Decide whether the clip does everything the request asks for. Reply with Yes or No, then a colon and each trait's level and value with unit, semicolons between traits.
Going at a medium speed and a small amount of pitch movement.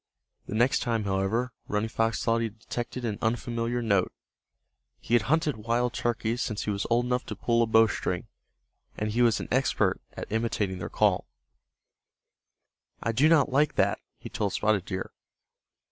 Yes: average, 165 wpm; narrow, 2.3 semitones